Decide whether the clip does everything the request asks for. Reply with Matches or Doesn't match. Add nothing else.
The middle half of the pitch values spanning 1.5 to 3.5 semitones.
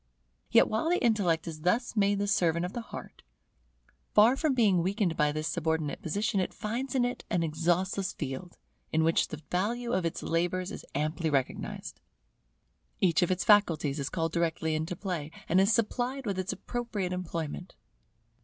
Doesn't match